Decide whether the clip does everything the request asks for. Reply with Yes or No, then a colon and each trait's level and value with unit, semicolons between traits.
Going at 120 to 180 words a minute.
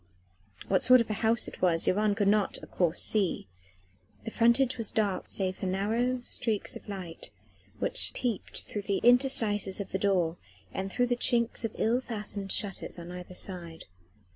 Yes: average, 175 wpm